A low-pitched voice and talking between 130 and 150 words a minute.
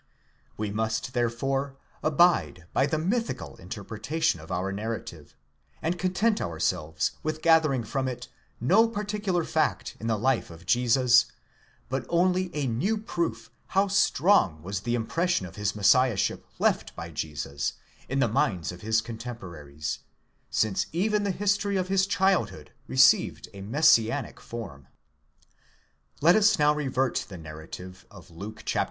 Yes: low, 120 Hz; average, 145 wpm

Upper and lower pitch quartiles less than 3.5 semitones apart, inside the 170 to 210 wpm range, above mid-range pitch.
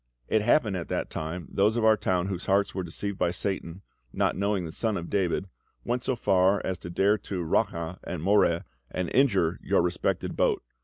No: average, 2.9 semitones; average, 200 wpm; very low, 95 Hz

